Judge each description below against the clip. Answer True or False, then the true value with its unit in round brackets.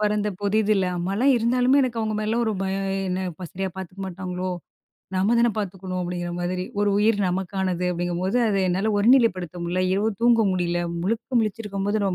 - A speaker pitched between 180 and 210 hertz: True (195 Hz)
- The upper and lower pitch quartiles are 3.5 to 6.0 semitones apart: False (3.1 semitones)